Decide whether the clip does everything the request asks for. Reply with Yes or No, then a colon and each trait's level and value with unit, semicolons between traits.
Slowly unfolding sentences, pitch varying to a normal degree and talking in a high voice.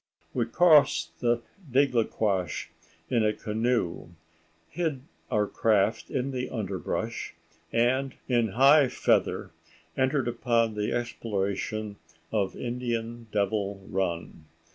No: slow, 100 wpm; average, 3.4 semitones; low, 115 Hz